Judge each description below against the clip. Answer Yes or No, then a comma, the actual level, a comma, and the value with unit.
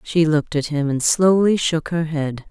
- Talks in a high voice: No, medium, 160 Hz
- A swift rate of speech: Yes, fast, 215 wpm